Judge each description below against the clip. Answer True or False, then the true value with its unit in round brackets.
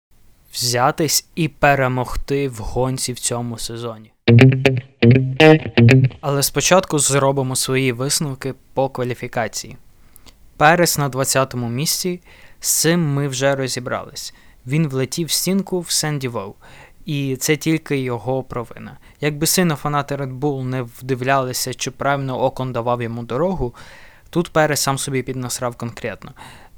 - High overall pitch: False (135 Hz)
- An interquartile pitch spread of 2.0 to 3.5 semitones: True (3.0 semitones)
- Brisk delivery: False (125 wpm)